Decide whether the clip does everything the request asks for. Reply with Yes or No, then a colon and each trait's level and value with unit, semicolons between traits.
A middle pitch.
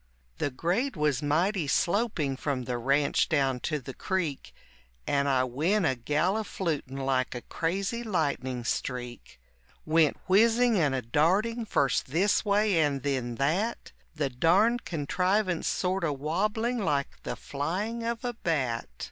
Yes: medium, 155 Hz